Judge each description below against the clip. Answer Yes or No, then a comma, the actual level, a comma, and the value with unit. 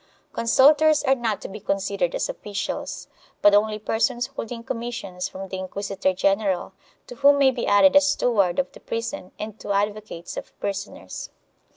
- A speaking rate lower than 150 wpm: No, average, 175 wpm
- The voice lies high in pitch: Yes, high, 215 Hz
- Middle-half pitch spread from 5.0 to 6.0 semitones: No, average, 4.0 semitones